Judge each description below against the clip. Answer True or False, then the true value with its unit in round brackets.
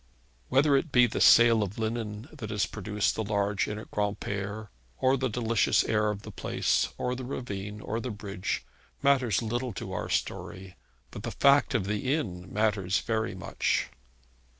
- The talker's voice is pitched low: True (110 Hz)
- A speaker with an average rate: True (175 wpm)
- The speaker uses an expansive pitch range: False (3.2 semitones)